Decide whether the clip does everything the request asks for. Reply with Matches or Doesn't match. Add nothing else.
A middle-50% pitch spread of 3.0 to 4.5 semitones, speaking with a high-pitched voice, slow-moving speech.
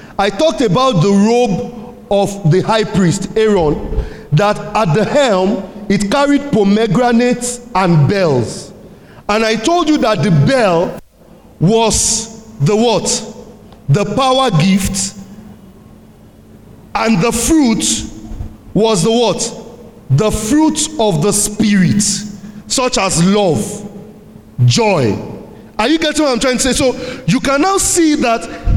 Matches